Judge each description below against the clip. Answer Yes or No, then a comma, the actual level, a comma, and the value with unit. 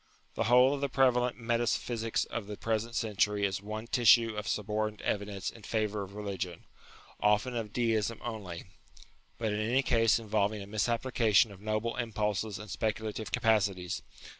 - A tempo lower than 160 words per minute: No, average, 165 wpm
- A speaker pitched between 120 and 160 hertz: No, low, 110 Hz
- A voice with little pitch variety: Yes, narrow, 2.0 semitones